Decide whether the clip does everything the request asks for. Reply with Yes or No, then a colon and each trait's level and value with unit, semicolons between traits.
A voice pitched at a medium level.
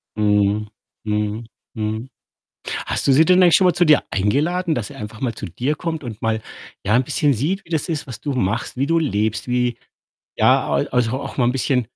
No: low, 125 Hz